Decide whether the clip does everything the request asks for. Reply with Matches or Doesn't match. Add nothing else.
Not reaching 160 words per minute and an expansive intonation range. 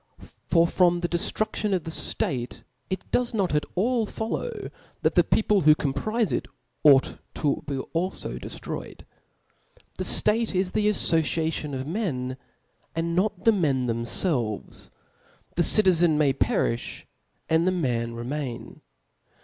Matches